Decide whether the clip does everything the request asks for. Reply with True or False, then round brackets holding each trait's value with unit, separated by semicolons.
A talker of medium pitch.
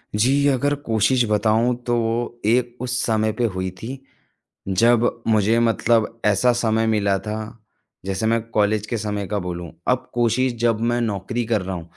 False (110 Hz)